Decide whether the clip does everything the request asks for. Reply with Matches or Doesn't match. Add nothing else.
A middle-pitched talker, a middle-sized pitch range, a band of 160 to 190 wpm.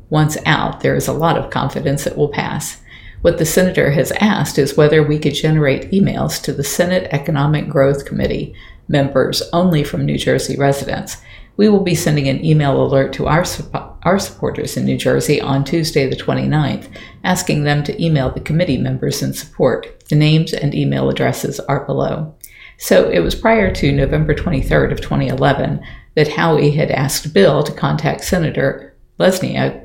Matches